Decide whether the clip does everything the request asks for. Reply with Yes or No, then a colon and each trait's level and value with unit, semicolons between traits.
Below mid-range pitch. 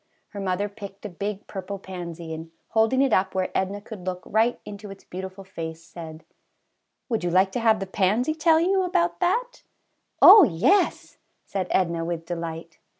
No: high, 195 Hz